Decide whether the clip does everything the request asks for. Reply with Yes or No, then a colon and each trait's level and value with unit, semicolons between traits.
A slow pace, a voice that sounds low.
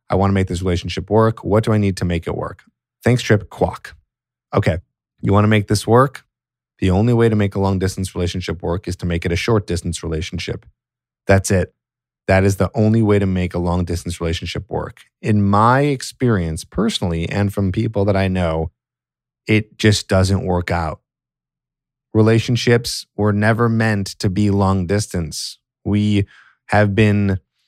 No: average, 180 wpm; low, 100 Hz